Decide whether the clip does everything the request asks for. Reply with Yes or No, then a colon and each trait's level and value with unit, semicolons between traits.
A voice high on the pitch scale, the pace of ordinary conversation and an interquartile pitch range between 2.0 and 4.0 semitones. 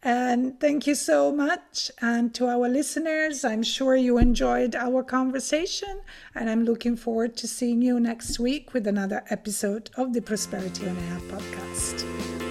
Yes: high, 245 Hz; average, 160 wpm; average, 3.0 semitones